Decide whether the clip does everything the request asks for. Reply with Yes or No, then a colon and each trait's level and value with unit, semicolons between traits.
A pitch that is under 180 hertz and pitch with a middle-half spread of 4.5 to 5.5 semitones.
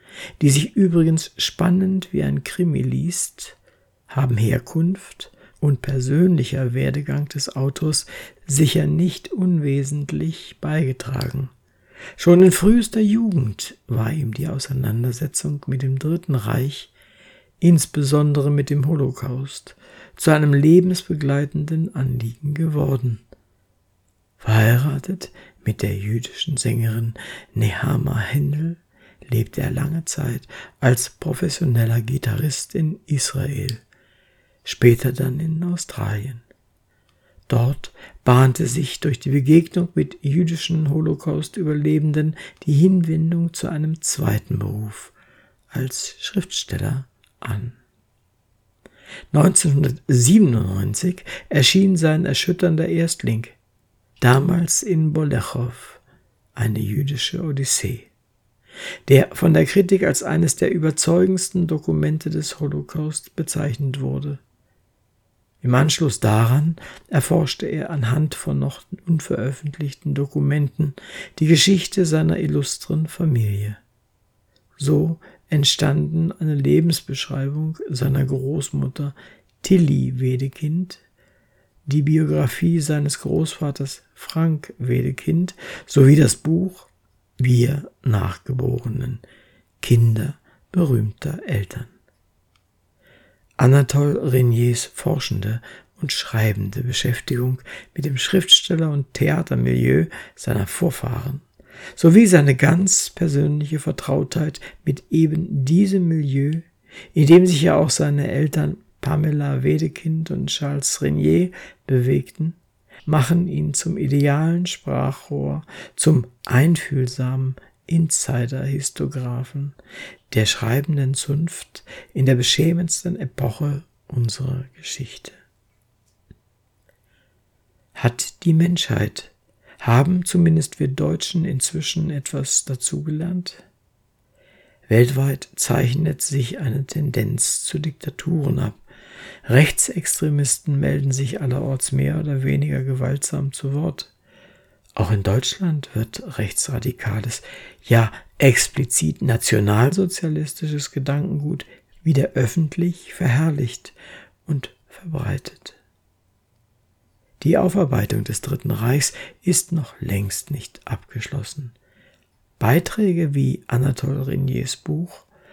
Yes: medium, 140 Hz; average, 4.8 semitones